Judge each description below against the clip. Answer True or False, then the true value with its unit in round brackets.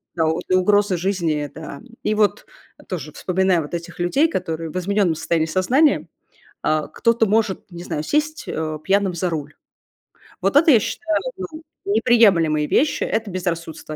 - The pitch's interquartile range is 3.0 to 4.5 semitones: False (5.0 semitones)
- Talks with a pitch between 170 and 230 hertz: True (185 Hz)